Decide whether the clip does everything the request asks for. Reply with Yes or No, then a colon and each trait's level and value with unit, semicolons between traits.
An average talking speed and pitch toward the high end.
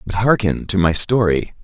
No: average, 185 wpm; low, 100 Hz